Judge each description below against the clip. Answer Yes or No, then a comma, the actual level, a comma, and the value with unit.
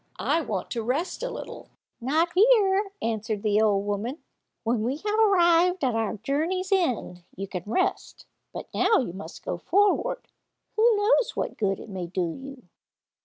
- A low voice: No, very high, 265 Hz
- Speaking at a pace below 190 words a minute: Yes, average, 170 wpm